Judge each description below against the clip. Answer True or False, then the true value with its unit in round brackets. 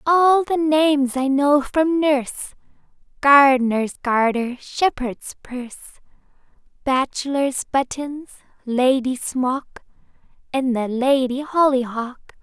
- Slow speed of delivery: True (90 wpm)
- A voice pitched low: False (270 Hz)